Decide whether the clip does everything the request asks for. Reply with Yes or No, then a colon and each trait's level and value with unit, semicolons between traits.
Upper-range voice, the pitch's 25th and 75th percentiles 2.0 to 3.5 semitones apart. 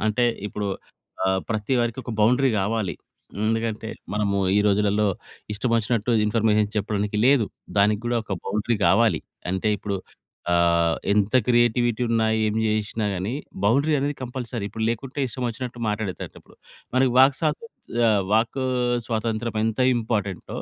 No: low, 110 Hz; narrow, 2.5 semitones